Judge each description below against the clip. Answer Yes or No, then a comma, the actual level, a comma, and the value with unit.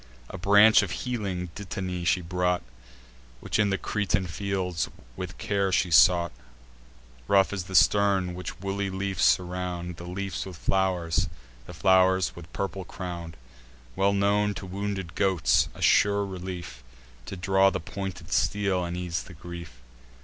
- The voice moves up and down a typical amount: No, narrow, 2.0 semitones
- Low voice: Yes, very low, 95 Hz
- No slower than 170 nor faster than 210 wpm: No, average, 150 wpm